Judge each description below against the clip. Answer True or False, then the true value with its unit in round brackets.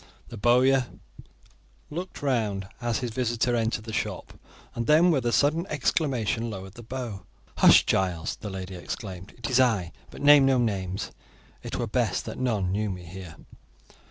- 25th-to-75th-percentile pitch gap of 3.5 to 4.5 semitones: False (5.1 semitones)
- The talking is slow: False (165 wpm)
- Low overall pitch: True (115 Hz)